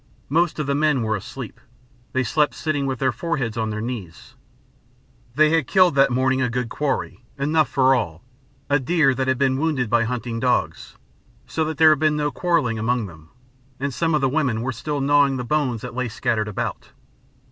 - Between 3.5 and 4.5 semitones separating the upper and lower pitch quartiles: Yes, average, 4.0 semitones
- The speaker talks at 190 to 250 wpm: Yes, average, 200 wpm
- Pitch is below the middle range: Yes, low, 130 Hz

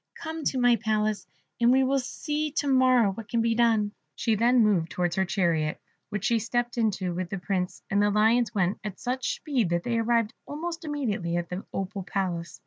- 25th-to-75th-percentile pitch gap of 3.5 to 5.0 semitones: Yes, average, 4.4 semitones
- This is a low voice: No, high, 220 Hz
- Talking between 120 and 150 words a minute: No, fast, 205 wpm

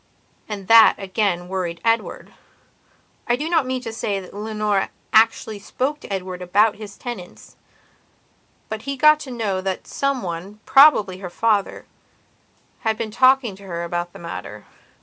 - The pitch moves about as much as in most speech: Yes, average, 4.2 semitones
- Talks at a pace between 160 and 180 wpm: No, average, 150 wpm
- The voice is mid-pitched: No, high, 210 Hz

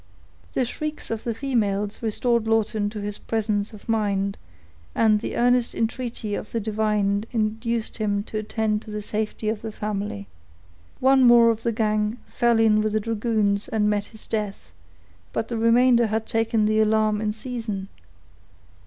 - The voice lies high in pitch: Yes, high, 220 Hz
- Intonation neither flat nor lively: No, narrow, 1.5 semitones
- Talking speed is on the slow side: No, average, 165 wpm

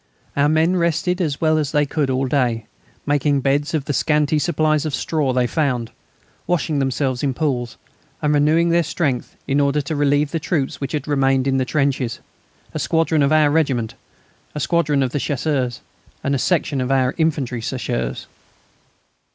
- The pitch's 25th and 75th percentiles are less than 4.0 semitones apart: Yes, average, 2.7 semitones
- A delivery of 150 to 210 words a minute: Yes, average, 175 wpm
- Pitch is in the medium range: Yes, medium, 145 Hz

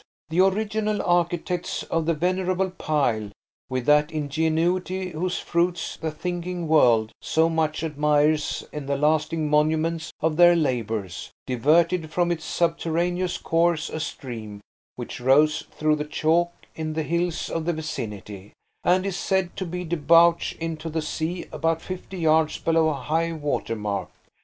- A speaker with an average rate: Yes, average, 145 wpm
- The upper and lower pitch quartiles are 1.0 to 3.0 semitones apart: Yes, narrow, 2.4 semitones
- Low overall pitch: No, medium, 160 Hz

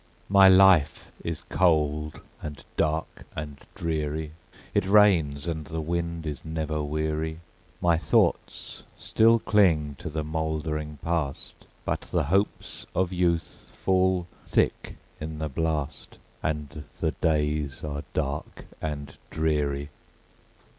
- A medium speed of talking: No, slow, 120 wpm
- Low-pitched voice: Yes, very low, 80 Hz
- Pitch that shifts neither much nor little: No, narrow, 2.0 semitones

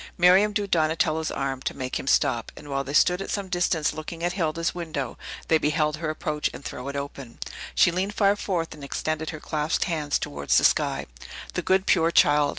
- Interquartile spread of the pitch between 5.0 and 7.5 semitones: No, average, 3.4 semitones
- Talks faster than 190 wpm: Yes, fast, 205 wpm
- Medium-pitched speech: Yes, medium, 155 Hz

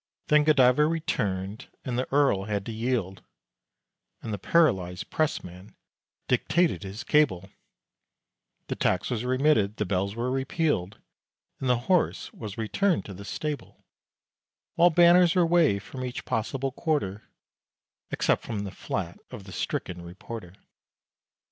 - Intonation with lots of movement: Yes, wide, 7.4 semitones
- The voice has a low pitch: Yes, low, 120 Hz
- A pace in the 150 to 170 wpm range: No, slow, 135 wpm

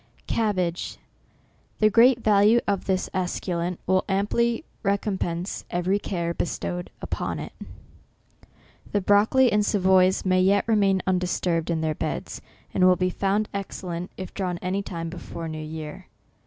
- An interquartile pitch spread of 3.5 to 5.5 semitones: No, narrow, 2.5 semitones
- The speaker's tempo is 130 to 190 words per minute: Yes, average, 140 wpm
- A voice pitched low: No, medium, 185 Hz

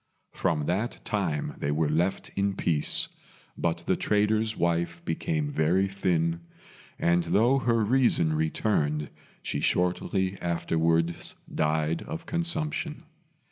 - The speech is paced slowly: Yes, slow, 115 wpm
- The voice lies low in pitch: Yes, very low, 90 Hz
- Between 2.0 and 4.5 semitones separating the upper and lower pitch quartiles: No, average, 4.9 semitones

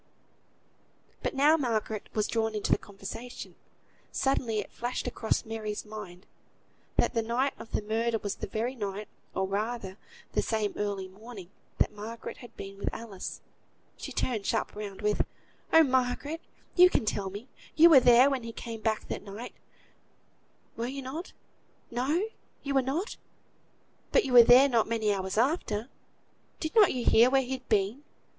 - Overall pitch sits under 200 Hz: No, high, 230 Hz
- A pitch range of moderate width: Yes, average, 3.7 semitones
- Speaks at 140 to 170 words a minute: Yes, average, 165 wpm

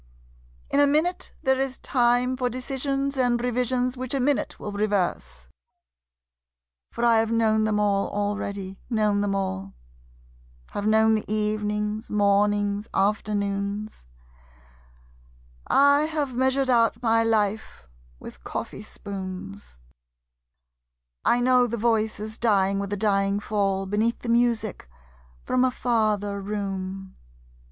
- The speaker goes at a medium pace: No, slow, 120 wpm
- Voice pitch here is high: Yes, high, 215 Hz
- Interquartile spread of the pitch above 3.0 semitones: Yes, average, 3.4 semitones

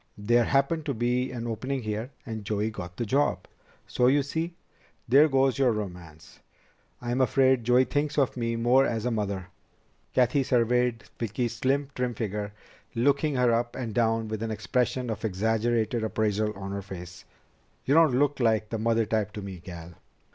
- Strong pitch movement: No, average, 3.4 semitones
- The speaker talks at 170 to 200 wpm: Yes, average, 175 wpm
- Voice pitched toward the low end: Yes, low, 115 Hz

